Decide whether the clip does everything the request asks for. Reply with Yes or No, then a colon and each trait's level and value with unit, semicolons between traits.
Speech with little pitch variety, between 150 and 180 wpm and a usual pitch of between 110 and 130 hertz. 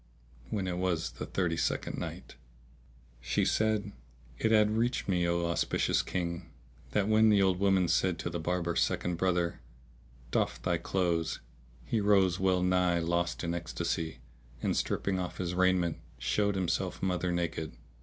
No: narrow, 2.1 semitones; average, 155 wpm; very low, 90 Hz